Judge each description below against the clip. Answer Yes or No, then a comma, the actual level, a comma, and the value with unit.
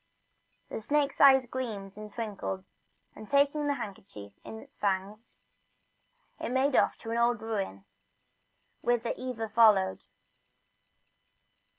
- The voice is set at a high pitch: Yes, high, 225 Hz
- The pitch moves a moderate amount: Yes, average, 4.4 semitones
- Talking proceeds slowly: Yes, slow, 115 wpm